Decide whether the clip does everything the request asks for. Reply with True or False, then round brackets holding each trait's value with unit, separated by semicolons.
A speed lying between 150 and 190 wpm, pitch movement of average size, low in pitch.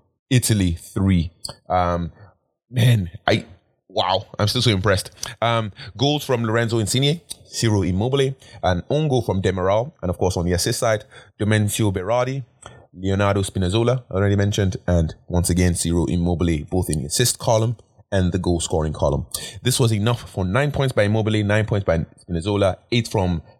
True (165 wpm; 4.5 semitones; 105 Hz)